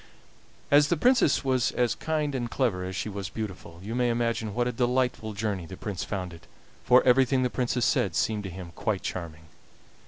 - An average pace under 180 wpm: No, average, 195 wpm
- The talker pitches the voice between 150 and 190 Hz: No, low, 115 Hz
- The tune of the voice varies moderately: Yes, average, 5.0 semitones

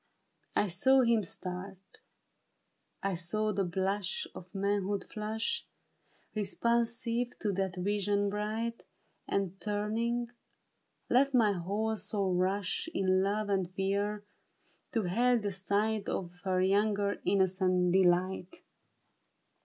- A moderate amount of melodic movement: No, narrow, 2.3 semitones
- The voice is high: Yes, high, 200 Hz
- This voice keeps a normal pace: No, slow, 110 wpm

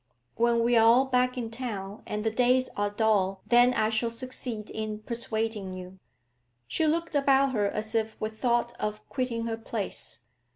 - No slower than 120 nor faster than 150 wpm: No, average, 175 wpm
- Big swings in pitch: No, average, 2.8 semitones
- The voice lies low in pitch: No, high, 225 Hz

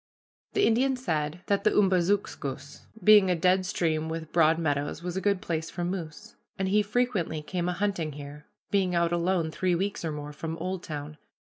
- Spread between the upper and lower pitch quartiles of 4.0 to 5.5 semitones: No, average, 3.5 semitones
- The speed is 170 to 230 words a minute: Yes, average, 180 wpm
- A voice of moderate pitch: Yes, medium, 175 Hz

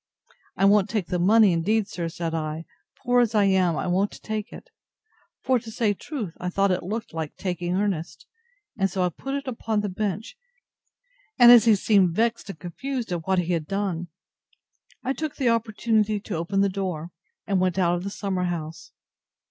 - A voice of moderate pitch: No, high, 195 Hz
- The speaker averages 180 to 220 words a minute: Yes, average, 195 wpm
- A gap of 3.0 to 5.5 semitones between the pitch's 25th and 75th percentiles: Yes, average, 3.9 semitones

